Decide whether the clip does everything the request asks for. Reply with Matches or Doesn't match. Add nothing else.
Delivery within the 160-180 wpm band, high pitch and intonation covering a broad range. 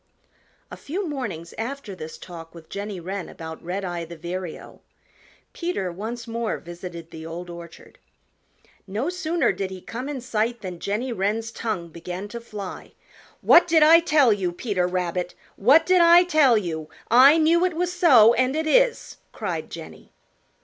Matches